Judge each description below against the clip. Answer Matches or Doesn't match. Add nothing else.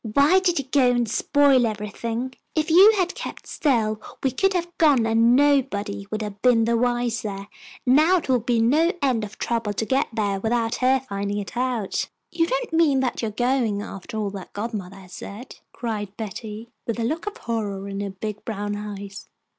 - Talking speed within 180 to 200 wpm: Matches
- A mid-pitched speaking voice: Doesn't match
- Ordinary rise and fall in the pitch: Matches